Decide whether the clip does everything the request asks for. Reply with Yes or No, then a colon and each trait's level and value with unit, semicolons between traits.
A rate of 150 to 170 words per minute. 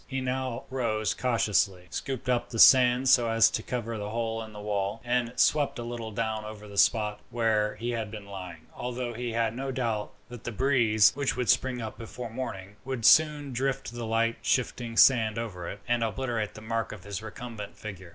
No: average, 200 wpm